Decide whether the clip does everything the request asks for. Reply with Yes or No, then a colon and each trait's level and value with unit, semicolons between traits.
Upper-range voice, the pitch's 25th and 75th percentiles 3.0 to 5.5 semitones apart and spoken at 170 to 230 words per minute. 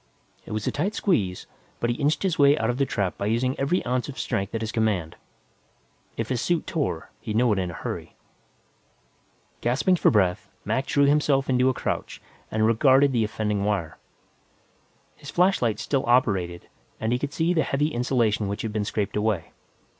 No: low, 120 Hz; average, 5.0 semitones; average, 190 wpm